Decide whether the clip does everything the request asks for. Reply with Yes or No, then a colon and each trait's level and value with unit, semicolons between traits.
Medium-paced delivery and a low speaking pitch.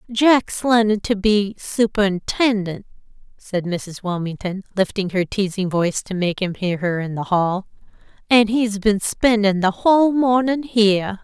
No: average, 150 wpm; high, 205 Hz